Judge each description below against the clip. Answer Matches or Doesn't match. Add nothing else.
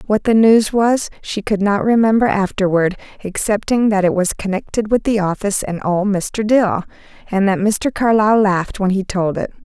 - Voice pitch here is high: Matches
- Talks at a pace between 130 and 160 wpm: Doesn't match